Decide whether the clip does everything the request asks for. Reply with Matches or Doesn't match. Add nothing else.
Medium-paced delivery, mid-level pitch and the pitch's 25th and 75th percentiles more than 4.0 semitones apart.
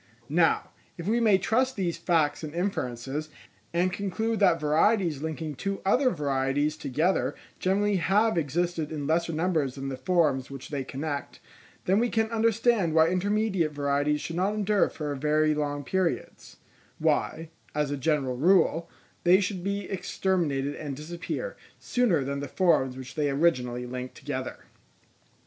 Matches